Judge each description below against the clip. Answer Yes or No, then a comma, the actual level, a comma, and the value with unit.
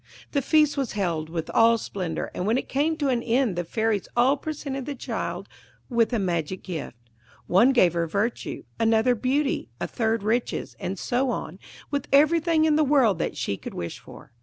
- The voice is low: No, high, 235 Hz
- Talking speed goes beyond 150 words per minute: Yes, average, 190 wpm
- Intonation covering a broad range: Yes, wide, 6.6 semitones